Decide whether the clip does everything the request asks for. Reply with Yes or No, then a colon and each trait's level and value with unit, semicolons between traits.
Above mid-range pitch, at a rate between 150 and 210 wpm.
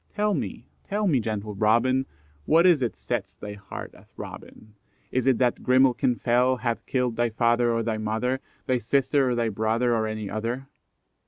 No: low, 120 Hz; average, 180 wpm